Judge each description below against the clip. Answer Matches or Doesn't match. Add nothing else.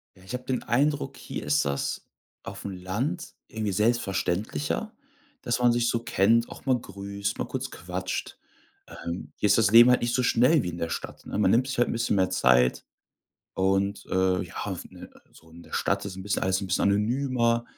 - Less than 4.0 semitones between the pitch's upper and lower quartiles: Doesn't match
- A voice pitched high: Doesn't match